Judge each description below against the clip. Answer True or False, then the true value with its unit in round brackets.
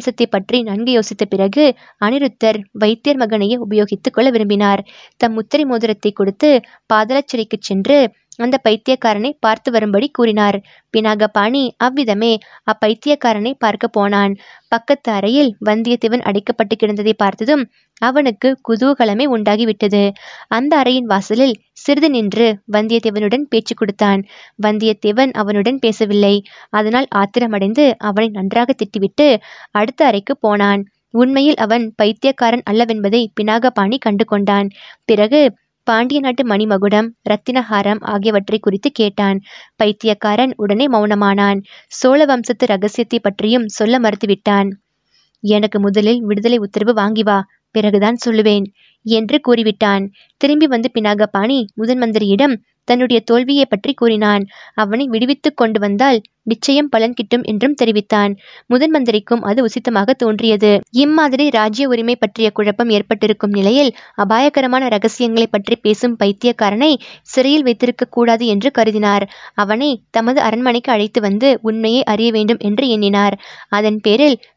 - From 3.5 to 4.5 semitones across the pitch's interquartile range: False (2.9 semitones)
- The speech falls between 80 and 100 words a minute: False (110 wpm)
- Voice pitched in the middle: False (225 Hz)